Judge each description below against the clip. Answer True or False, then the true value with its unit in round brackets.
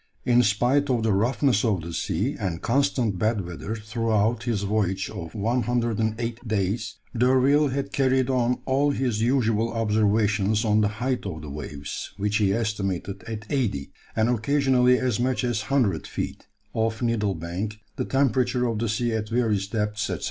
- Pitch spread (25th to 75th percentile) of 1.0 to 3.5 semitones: True (3.2 semitones)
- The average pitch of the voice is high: False (110 Hz)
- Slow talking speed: False (165 wpm)